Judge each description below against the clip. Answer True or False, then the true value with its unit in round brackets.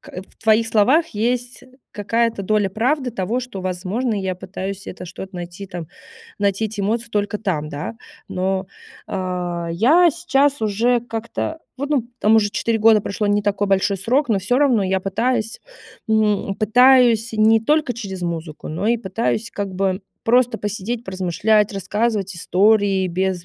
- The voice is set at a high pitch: True (210 Hz)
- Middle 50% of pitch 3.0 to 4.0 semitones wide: True (3.5 semitones)